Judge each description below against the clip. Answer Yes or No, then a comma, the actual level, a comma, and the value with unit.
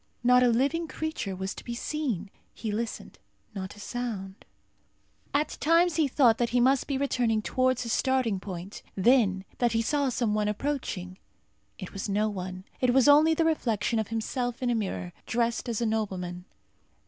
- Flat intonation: No, average, 4.4 semitones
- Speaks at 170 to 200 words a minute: Yes, average, 180 wpm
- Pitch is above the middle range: Yes, high, 235 Hz